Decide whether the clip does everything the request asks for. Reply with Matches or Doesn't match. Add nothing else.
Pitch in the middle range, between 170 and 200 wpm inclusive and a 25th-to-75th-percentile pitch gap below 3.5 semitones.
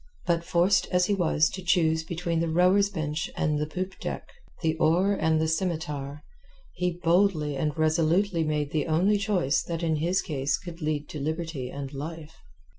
Matches